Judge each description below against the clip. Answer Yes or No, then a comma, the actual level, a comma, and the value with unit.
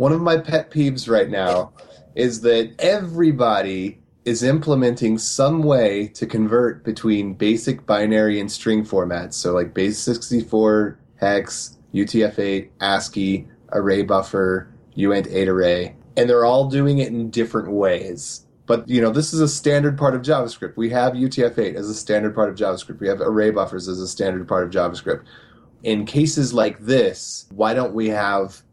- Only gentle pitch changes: No, average, 4.0 semitones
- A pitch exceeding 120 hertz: No, low, 110 Hz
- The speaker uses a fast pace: No, average, 160 wpm